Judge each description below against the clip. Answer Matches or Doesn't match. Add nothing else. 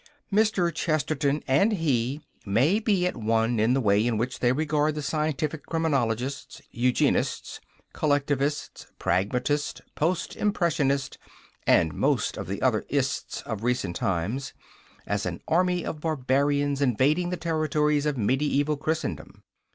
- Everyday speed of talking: Doesn't match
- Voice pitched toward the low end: Doesn't match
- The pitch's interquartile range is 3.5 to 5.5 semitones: Matches